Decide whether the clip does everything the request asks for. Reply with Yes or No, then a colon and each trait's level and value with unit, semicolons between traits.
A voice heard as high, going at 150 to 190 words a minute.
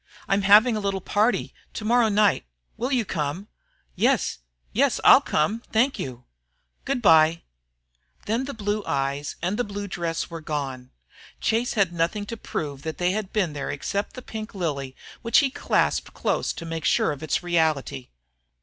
Yes: high, 195 Hz; average, 170 wpm